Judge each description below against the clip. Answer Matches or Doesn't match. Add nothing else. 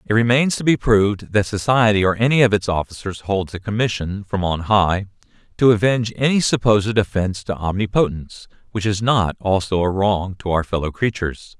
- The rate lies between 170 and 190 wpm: Matches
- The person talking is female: Doesn't match